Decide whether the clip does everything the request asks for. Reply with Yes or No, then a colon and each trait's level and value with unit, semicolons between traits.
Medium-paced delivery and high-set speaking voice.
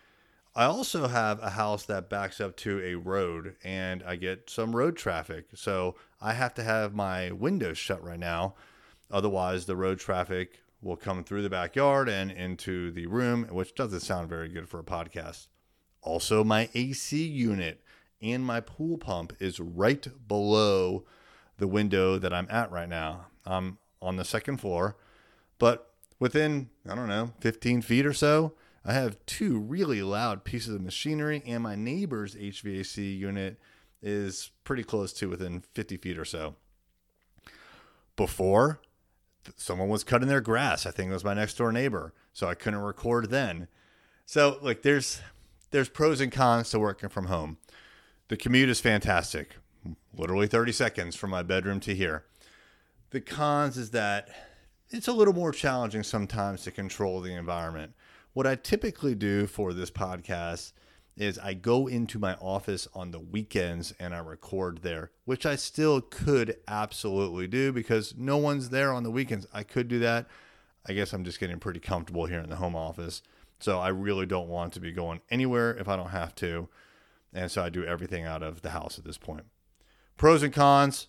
No: average, 175 wpm; low, 100 Hz